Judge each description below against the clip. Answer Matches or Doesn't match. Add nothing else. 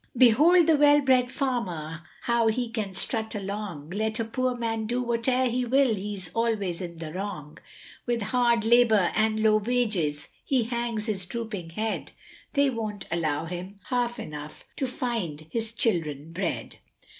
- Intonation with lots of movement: Doesn't match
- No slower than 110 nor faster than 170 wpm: Matches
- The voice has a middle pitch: Doesn't match